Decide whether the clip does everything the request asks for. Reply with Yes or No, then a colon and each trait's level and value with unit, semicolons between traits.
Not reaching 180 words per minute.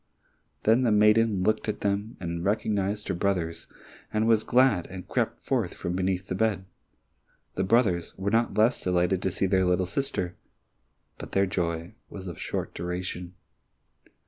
Yes: average, 155 wpm